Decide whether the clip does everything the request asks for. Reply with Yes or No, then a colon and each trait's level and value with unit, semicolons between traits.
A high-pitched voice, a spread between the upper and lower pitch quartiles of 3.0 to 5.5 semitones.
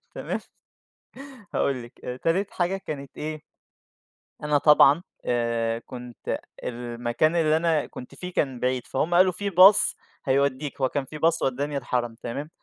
No: medium, 140 Hz; average, 4.6 semitones